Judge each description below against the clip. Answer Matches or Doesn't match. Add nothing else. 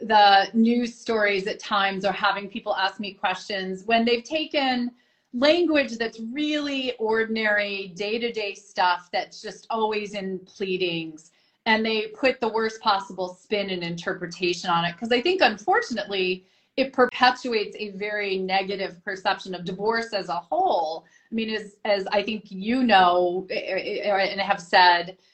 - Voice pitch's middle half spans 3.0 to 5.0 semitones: Matches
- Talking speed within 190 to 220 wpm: Doesn't match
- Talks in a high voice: Matches